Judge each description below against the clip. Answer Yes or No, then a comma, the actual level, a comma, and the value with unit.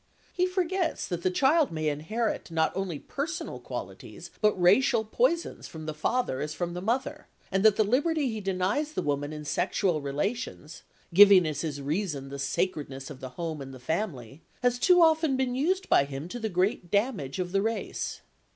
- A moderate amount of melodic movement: No, wide, 8.5 semitones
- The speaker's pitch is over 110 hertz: Yes, high, 190 Hz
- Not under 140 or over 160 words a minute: No, average, 190 wpm